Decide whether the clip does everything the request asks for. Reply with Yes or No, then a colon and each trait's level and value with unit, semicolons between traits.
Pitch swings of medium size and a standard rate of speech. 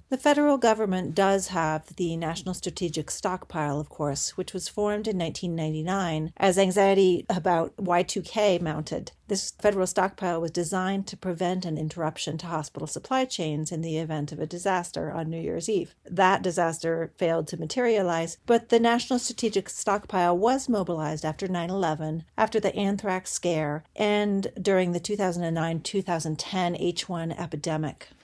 Yes: average, 3.3 semitones; average, 150 wpm